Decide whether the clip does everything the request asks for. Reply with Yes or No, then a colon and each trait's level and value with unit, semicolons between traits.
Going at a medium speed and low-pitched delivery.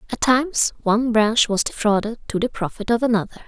No: average, 190 wpm; high, 225 Hz